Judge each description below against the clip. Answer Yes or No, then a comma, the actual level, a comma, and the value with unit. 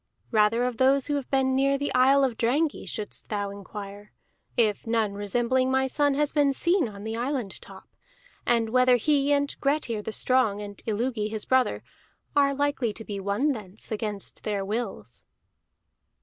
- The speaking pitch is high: Yes, high, 240 Hz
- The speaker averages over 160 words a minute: Yes, average, 170 wpm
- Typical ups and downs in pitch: Yes, average, 4.6 semitones